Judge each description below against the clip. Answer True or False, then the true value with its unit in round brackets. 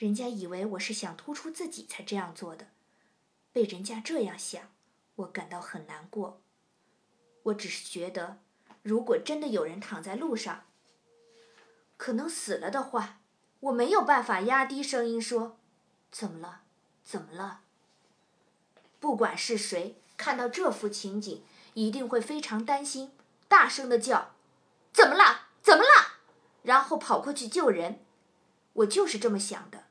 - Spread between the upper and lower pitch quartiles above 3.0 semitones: True (5.1 semitones)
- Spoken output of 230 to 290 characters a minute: False (215 characters per minute)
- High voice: True (230 Hz)